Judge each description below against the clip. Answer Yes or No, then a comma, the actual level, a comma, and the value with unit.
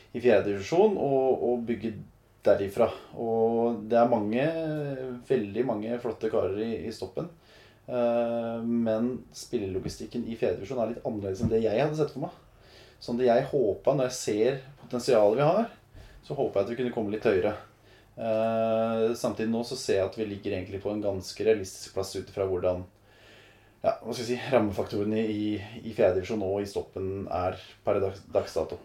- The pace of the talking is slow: No, average, 175 wpm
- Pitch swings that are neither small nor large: Yes, average, 3.3 semitones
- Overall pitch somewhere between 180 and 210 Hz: No, low, 110 Hz